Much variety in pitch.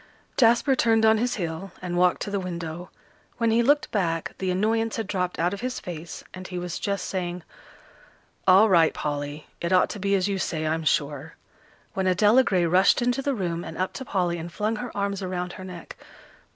No: average, 3.8 semitones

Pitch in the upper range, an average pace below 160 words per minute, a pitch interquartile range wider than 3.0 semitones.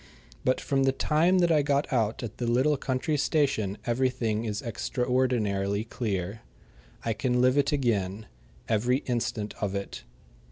No: low, 125 Hz; average, 150 wpm; average, 4.0 semitones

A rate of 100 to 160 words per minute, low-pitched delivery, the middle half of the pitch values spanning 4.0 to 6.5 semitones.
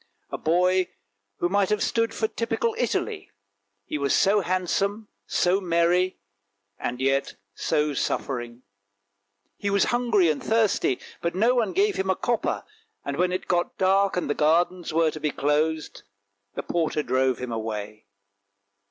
No: average, 150 wpm; medium, 175 Hz; average, 5.2 semitones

